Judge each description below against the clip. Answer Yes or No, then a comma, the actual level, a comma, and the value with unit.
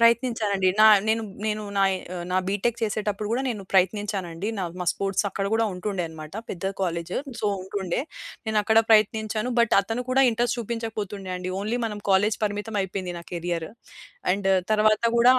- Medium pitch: No, high, 205 Hz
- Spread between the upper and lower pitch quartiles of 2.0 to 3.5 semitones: Yes, narrow, 2.6 semitones